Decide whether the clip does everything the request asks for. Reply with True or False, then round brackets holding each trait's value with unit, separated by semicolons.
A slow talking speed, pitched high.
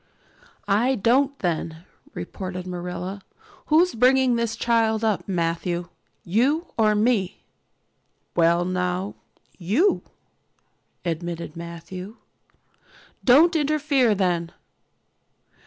True (85 wpm; 200 Hz)